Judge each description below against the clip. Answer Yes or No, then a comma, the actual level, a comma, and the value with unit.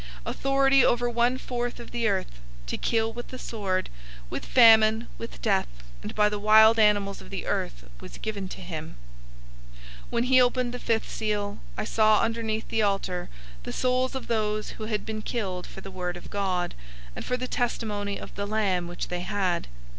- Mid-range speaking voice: No, high, 215 Hz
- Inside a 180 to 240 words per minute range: Yes, average, 190 wpm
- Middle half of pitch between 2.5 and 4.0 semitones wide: Yes, average, 3.4 semitones